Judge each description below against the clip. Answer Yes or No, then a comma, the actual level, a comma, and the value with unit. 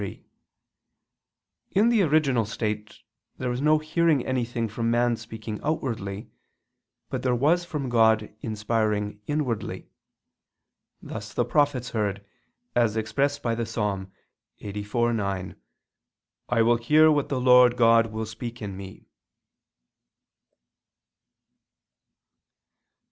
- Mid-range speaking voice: No, low, 115 Hz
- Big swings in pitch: No, average, 3.7 semitones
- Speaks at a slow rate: Yes, slow, 110 wpm